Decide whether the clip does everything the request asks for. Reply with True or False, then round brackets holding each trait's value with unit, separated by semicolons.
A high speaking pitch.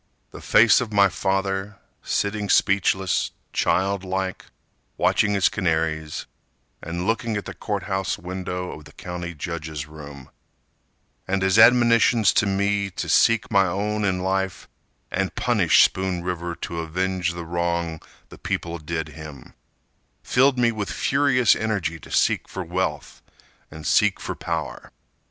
False (95 Hz)